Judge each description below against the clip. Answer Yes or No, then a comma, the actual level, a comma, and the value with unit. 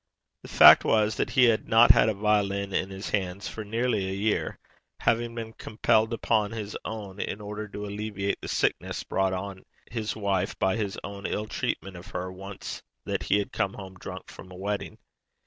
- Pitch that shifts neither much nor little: No, narrow, 2.1 semitones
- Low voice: Yes, low, 105 Hz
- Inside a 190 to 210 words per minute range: Yes, average, 195 wpm